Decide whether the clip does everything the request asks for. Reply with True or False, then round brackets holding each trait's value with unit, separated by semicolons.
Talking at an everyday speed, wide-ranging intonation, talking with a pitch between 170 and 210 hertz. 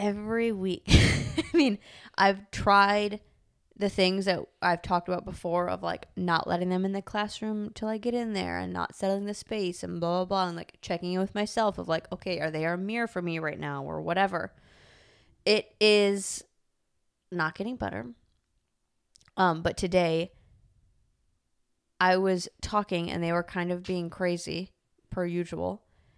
False (170 wpm; 3.2 semitones; 185 Hz)